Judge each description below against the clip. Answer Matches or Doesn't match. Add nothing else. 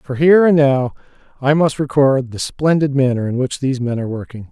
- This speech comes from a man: Matches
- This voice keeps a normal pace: Doesn't match